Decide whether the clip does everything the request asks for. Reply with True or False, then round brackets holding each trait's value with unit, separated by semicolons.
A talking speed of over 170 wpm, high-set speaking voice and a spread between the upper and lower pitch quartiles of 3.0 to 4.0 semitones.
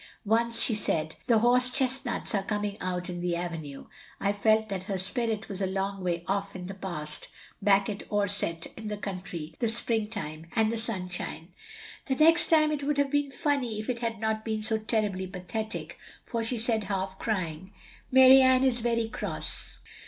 True (190 wpm; 215 Hz; 3.7 semitones)